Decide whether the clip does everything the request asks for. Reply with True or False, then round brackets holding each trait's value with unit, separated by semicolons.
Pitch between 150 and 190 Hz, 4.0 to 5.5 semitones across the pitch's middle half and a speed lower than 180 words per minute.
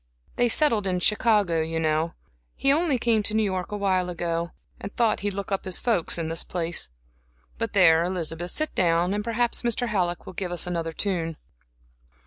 False (185 Hz; 4.3 semitones; 185 wpm)